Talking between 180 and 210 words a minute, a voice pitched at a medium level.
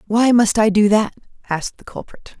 No: average, 200 wpm; high, 215 Hz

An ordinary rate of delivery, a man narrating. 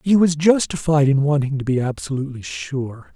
Yes: average, 170 wpm; male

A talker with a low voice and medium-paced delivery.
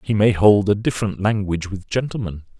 Yes: low, 100 Hz; average, 185 wpm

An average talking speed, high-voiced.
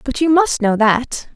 No: fast, 220 wpm; very high, 260 Hz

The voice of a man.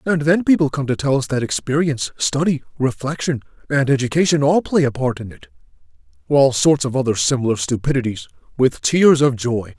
Yes: male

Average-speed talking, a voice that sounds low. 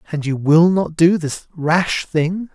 No: average, 190 wpm; medium, 165 Hz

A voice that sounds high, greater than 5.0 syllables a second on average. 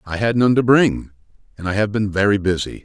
No: low, 105 Hz; 5.8 syllables/s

